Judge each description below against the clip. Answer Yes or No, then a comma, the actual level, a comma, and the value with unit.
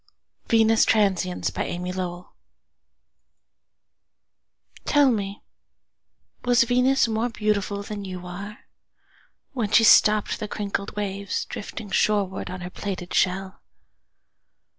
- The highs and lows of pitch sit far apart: No, average, 2.7 semitones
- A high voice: Yes, high, 205 Hz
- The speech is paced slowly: Yes, slow, 80 wpm